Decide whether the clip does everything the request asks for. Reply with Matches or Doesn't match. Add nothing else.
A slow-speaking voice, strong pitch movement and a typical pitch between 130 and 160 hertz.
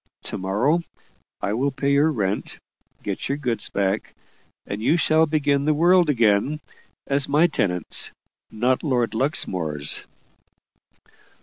Matches